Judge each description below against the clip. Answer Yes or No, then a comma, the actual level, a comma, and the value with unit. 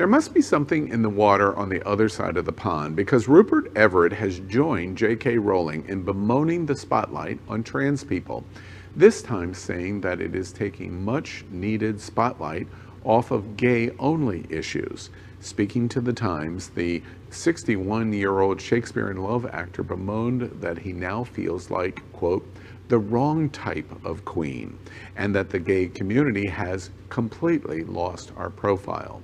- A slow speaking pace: No, average, 155 wpm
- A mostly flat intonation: No, average, 4.3 semitones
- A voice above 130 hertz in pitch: No, low, 105 Hz